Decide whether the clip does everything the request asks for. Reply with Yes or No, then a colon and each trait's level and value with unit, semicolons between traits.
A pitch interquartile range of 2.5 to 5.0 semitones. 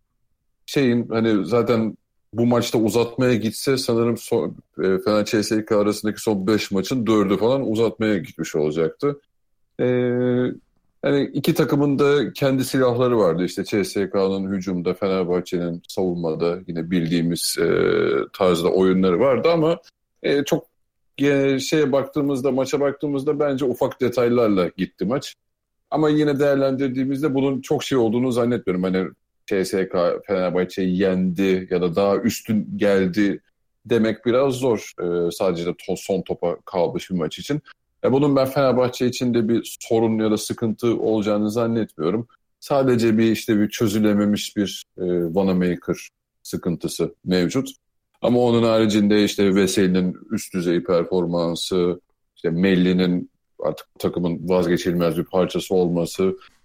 No: wide, 5.6 semitones